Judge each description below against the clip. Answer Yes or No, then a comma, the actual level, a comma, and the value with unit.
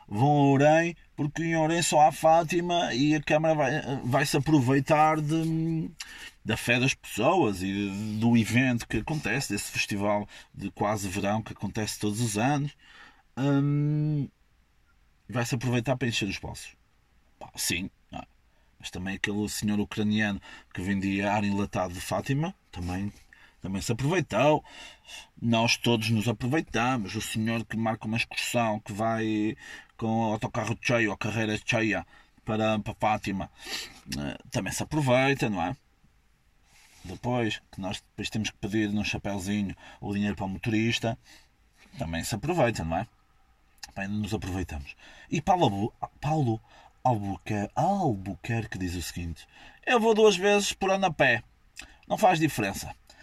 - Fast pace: No, average, 145 wpm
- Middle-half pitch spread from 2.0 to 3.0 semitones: No, wide, 5.5 semitones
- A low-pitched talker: Yes, low, 115 Hz